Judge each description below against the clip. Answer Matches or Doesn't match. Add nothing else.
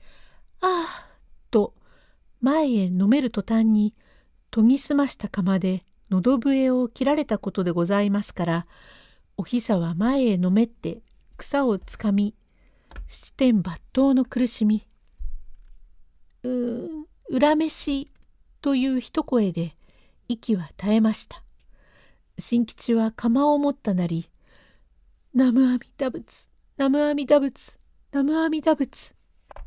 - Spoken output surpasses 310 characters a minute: Doesn't match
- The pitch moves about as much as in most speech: Doesn't match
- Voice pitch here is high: Matches